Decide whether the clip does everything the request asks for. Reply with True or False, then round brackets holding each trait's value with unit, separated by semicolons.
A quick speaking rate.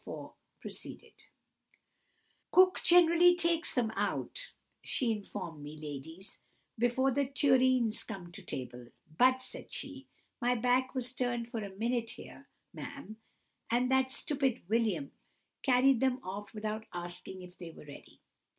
False (135 wpm)